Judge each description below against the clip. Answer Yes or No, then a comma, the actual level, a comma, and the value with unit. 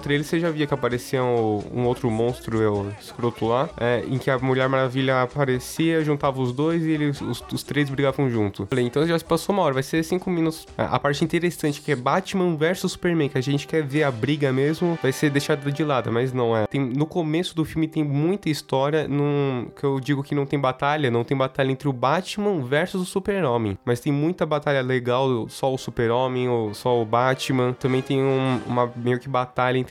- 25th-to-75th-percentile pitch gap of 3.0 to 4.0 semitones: Yes, average, 3.6 semitones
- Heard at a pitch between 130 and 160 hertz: Yes, medium, 140 Hz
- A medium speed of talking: No, fast, 220 wpm